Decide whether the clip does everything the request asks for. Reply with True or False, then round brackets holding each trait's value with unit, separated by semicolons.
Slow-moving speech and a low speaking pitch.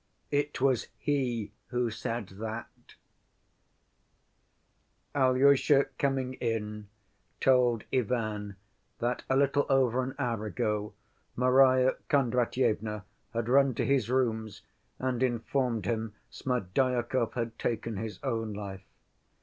True (105 wpm; 120 Hz)